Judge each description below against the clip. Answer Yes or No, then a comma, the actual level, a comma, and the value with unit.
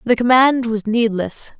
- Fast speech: No, average, 150 wpm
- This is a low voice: No, high, 235 Hz